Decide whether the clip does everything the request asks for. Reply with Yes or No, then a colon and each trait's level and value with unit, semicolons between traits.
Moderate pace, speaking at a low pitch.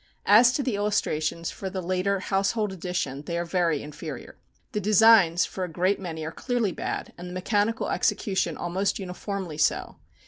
No: average, 170 wpm; medium, 185 Hz